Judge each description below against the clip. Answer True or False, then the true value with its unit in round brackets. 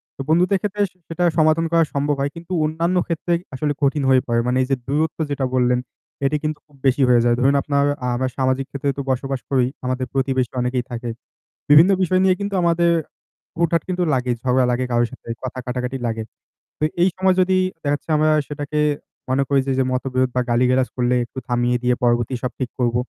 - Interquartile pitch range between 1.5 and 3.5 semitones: False (3.9 semitones)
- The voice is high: False (135 Hz)